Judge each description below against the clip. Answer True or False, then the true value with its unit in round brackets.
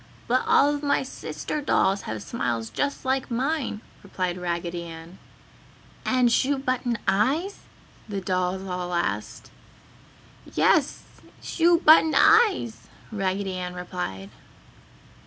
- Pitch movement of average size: False (7.4 semitones)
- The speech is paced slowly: True (115 wpm)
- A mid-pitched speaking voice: False (200 Hz)